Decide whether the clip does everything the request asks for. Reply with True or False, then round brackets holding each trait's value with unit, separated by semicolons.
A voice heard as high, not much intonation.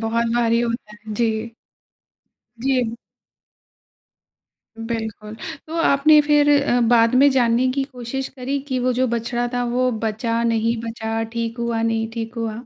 True (235 Hz; 1.9 semitones)